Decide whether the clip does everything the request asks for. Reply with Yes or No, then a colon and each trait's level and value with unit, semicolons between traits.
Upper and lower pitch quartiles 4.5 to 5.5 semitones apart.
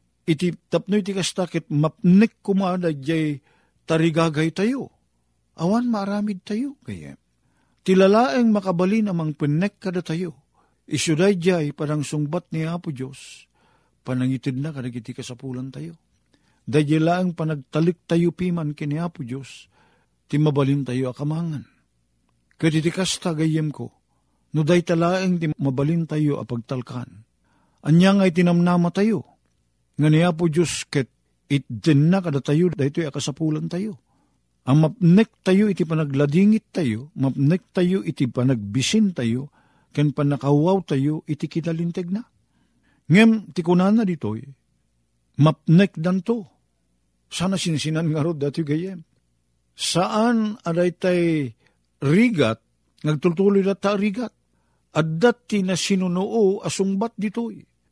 Yes: average, 4.9 semitones